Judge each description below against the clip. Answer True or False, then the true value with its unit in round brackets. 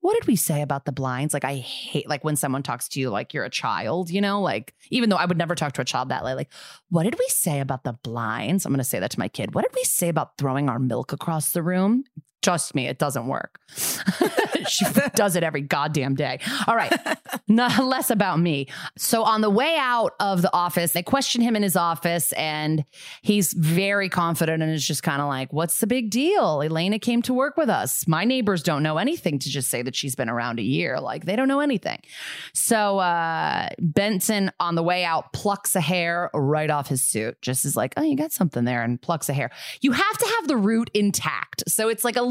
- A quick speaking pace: True (240 wpm)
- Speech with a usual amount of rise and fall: False (6.9 semitones)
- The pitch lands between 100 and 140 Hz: False (175 Hz)